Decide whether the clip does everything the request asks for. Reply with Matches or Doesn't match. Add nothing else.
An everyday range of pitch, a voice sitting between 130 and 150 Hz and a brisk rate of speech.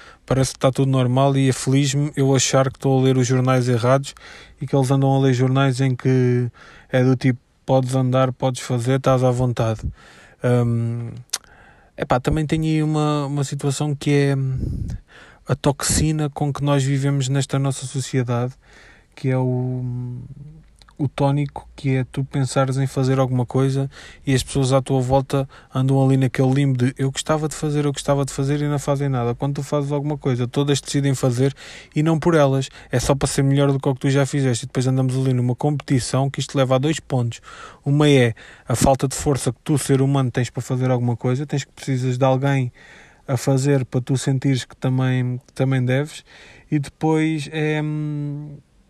Doesn't match